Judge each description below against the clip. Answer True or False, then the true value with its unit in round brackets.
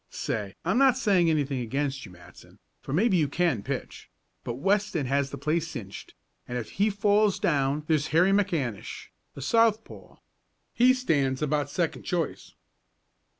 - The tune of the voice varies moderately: False (6.7 semitones)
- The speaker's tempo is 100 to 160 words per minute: True (150 wpm)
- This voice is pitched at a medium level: True (155 Hz)